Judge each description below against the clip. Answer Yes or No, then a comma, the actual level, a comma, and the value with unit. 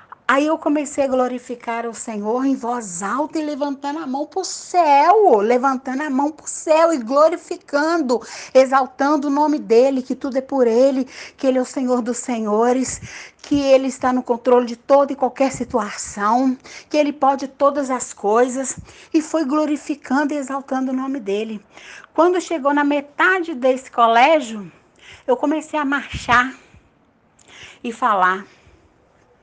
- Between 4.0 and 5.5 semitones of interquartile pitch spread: No, average, 3.2 semitones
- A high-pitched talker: Yes, very high, 270 Hz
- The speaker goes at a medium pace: Yes, average, 155 wpm